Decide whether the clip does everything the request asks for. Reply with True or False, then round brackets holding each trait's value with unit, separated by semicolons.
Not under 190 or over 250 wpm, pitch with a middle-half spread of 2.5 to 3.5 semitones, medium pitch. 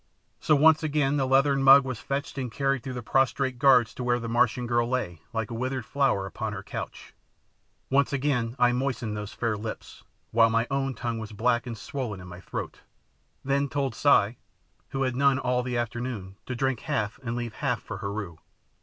False (200 wpm; 3.0 semitones; 125 Hz)